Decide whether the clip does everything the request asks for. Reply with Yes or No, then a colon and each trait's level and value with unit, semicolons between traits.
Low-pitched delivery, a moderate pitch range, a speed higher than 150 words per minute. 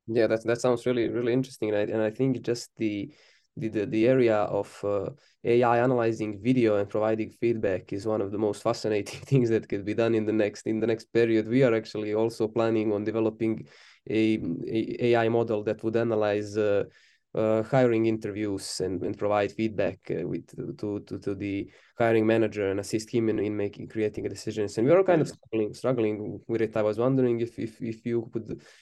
No: low, 110 Hz; narrow, 1.7 semitones; fast, 205 wpm